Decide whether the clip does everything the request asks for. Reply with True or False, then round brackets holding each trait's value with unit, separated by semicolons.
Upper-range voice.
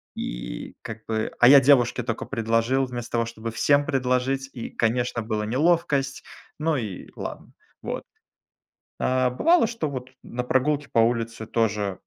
False (125 Hz)